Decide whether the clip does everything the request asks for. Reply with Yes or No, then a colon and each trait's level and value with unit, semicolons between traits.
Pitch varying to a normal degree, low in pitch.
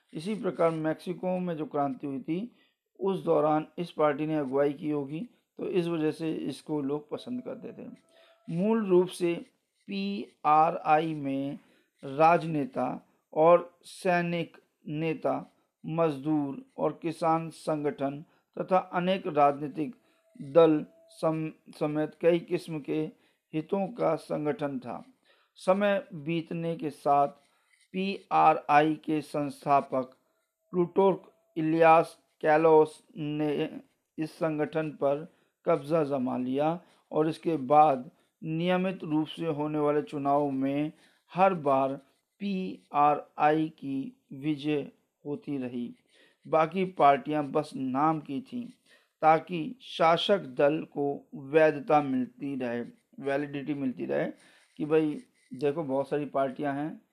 No: average, 3.6 semitones; medium, 155 Hz